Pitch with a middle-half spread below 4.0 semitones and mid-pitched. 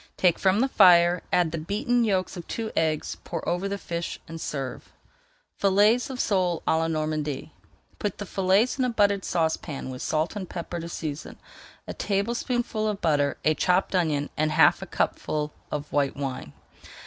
No: average, 4.6 semitones; medium, 175 Hz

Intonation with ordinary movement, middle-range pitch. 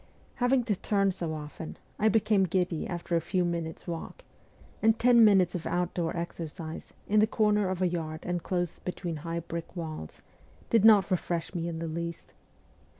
Yes: average, 3.1 semitones; medium, 175 Hz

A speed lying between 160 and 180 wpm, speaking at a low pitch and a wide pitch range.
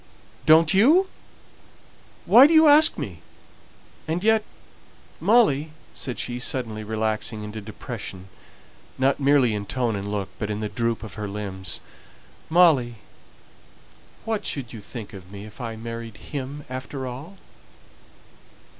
No: slow, 135 wpm; low, 120 Hz; wide, 6.6 semitones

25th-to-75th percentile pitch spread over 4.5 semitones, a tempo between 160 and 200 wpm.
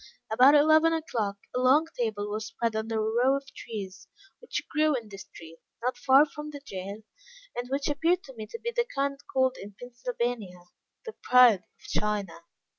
Yes: average, 5.3 semitones; average, 190 wpm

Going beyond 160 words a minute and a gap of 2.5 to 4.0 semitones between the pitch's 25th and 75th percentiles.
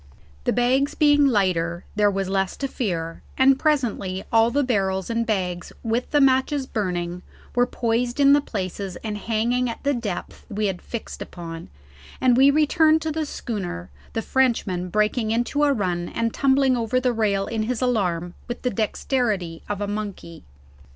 No: average, 175 wpm; average, 5.2 semitones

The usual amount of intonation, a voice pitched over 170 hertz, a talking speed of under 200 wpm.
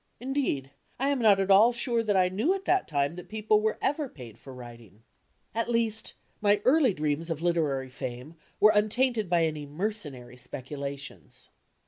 No: wide, 8.3 semitones; high, 190 Hz; average, 170 wpm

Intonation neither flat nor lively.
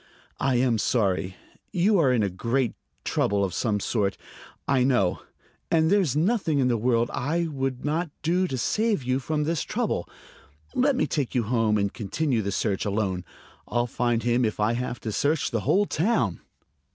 No: wide, 6.3 semitones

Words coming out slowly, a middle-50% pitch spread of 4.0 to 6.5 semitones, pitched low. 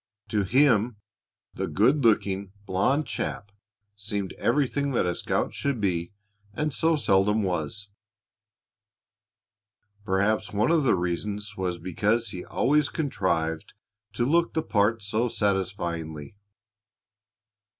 Yes: slow, 115 wpm; average, 4.6 semitones; low, 105 Hz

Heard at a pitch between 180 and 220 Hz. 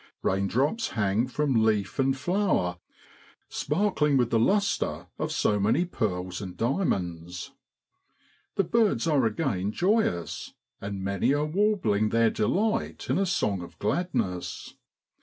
No: low, 115 Hz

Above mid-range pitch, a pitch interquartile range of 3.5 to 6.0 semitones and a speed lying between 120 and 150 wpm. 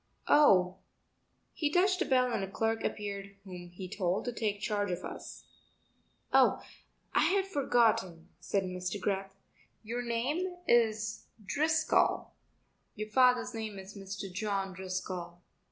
Yes: high, 205 Hz; average, 4.2 semitones; slow, 135 wpm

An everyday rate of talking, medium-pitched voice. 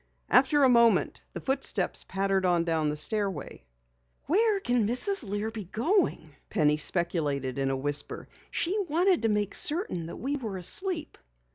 No: average, 155 wpm; high, 210 Hz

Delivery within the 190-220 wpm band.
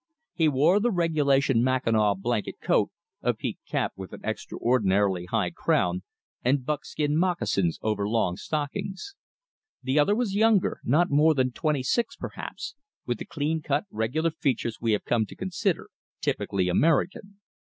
No: average, 150 wpm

